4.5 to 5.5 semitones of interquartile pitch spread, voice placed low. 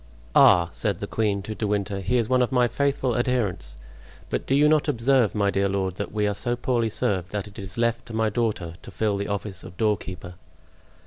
No: average, 3.5 semitones; low, 105 Hz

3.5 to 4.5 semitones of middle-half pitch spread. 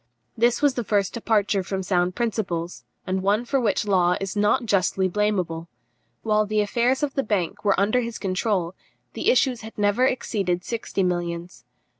Yes: average, 3.8 semitones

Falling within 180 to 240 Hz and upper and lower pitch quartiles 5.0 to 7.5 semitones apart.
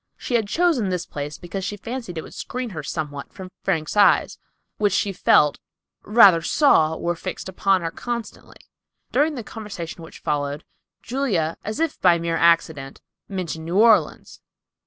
Yes: medium, 185 Hz; average, 5.3 semitones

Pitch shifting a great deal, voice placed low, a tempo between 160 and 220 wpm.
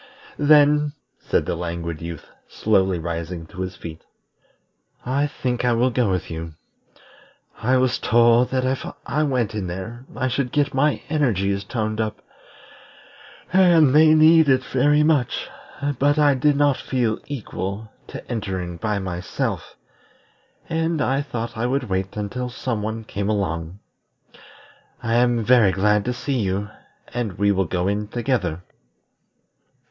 No: wide, 5.7 semitones; low, 115 Hz; average, 145 wpm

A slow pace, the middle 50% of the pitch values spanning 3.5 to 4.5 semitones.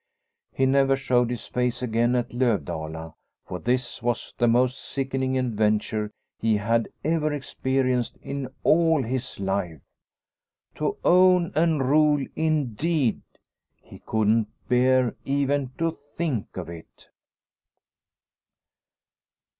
Yes: slow, 110 wpm; average, 3.9 semitones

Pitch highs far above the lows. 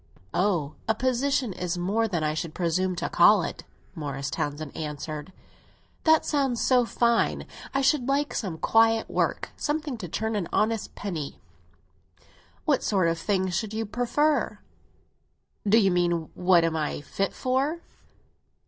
Yes: wide, 6.3 semitones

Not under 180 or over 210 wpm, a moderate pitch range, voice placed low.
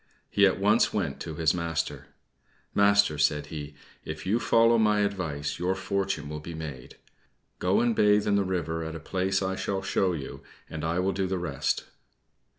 Yes: average, 185 wpm; average, 4.0 semitones; very low, 90 Hz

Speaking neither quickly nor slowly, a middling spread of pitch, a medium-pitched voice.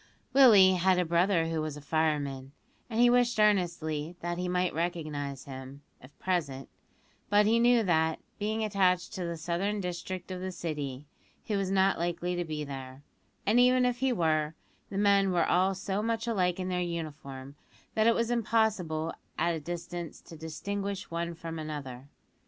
Yes: average, 175 wpm; average, 4.2 semitones; medium, 175 Hz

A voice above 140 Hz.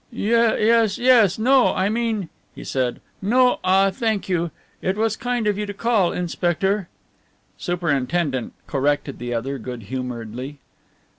Yes: high, 190 Hz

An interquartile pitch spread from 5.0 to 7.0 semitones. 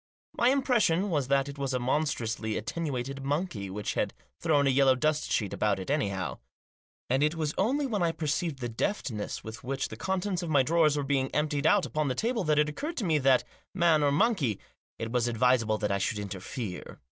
Yes: wide, 5.4 semitones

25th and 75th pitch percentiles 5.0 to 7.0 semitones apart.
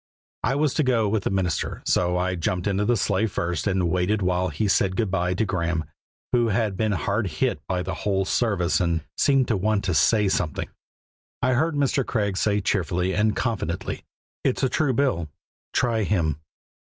No: average, 3.9 semitones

